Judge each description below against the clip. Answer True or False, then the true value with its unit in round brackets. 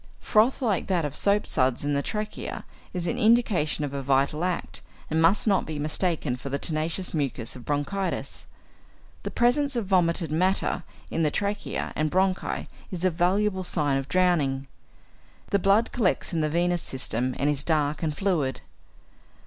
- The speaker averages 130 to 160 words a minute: False (170 wpm)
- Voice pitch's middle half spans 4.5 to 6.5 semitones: True (5.0 semitones)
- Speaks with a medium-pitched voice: True (170 Hz)